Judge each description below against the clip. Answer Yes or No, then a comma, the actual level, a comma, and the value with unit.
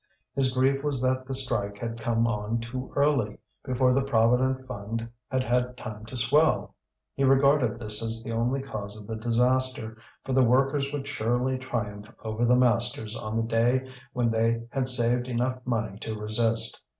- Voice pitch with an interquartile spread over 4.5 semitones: No, narrow, 2.4 semitones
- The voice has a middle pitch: No, low, 120 Hz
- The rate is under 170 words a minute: No, average, 175 wpm